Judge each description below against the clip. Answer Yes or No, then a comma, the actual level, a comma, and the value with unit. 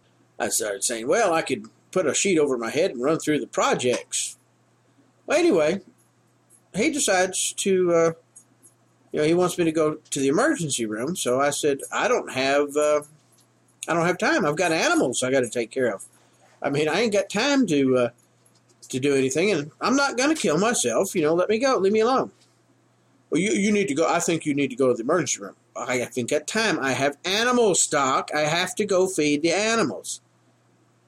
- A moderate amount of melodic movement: No, wide, 5.9 semitones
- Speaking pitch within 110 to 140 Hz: No, medium, 155 Hz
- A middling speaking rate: No, fast, 215 wpm